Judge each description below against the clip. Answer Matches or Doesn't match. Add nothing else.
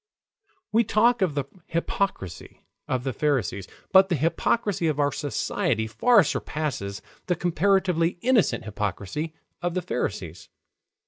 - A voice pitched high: Doesn't match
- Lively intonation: Matches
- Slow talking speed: Matches